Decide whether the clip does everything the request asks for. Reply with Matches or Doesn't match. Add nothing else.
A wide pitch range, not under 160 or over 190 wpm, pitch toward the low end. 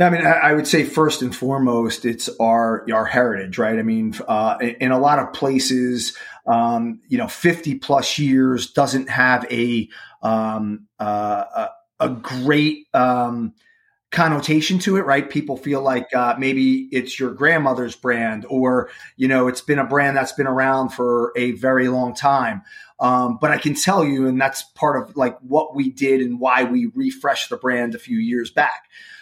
Doesn't match